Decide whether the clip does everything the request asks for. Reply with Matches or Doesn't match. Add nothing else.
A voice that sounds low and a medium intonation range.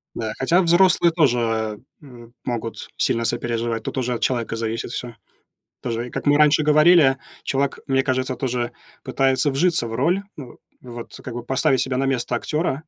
Matches